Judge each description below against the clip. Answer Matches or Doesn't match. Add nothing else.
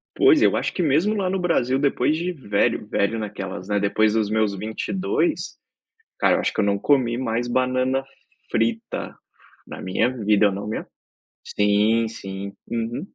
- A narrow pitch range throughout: Doesn't match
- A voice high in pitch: Doesn't match